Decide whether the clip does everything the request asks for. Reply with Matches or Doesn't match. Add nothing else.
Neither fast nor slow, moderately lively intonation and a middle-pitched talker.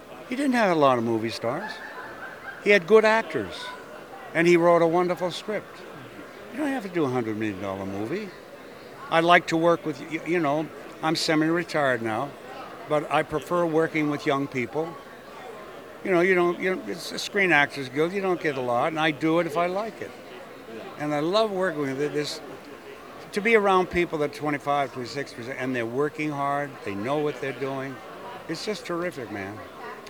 Matches